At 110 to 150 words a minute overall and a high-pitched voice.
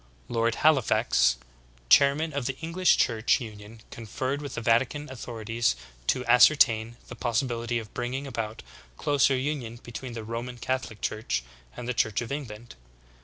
No: average, 145 wpm; low, 120 Hz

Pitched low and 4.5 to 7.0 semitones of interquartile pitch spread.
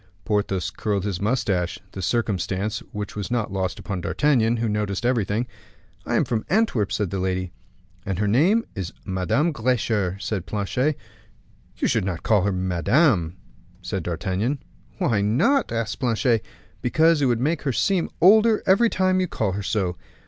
Yes: low, 105 Hz; wide, 5.5 semitones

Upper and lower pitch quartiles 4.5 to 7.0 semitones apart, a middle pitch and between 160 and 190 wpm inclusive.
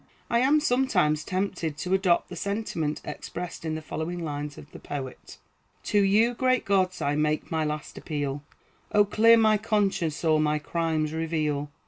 Yes: average, 5.2 semitones; medium, 165 Hz; average, 165 wpm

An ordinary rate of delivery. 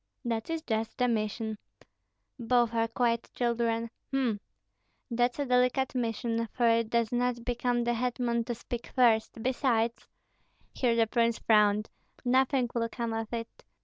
Yes: average, 150 wpm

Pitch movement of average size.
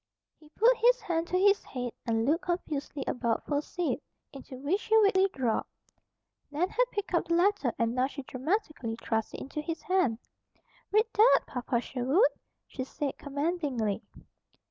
No: wide, 6.7 semitones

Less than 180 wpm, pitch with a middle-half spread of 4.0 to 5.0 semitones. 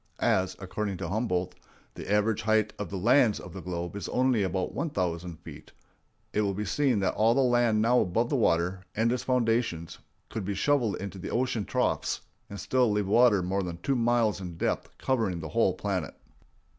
No: average, 195 wpm; average, 4.5 semitones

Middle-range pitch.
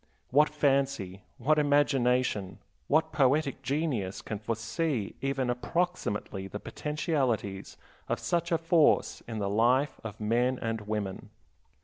No: low, 125 Hz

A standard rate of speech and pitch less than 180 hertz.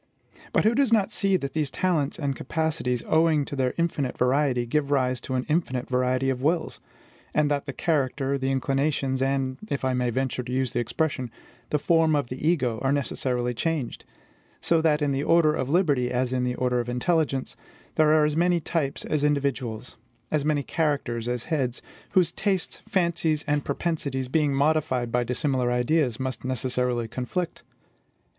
Yes: average, 180 wpm; medium, 140 Hz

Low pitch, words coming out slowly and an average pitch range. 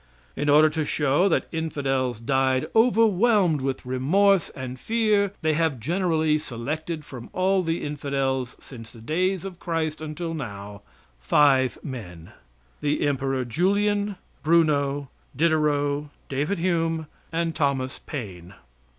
No: medium, 150 Hz; slow, 125 wpm; average, 4.2 semitones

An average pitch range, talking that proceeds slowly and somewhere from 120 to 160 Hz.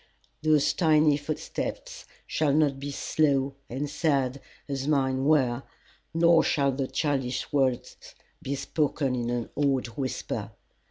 No: narrow, 2.3 semitones; slow, 125 wpm; medium, 140 Hz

